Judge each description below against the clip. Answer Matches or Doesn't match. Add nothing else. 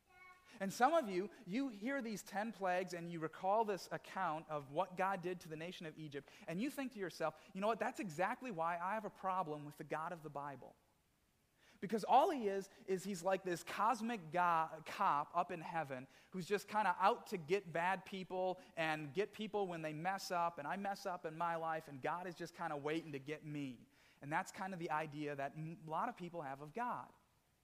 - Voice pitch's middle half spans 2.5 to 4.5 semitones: Matches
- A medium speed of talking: Doesn't match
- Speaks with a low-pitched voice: Doesn't match